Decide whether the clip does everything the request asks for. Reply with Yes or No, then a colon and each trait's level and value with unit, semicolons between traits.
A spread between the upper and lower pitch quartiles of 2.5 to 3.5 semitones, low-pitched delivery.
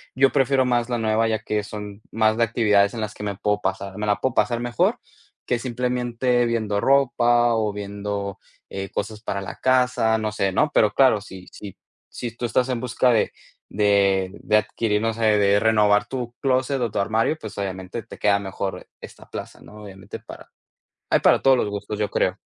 Yes: average, 2.9 semitones; low, 110 Hz